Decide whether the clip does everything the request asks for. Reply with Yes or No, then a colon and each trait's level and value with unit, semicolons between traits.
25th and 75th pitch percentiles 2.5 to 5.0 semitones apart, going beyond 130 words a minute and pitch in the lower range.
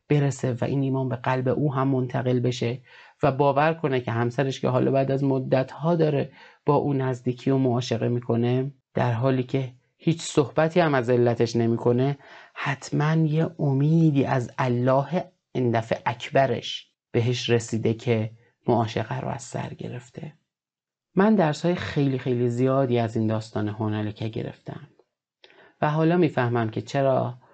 Yes: average, 3.2 semitones; average, 145 wpm; low, 130 Hz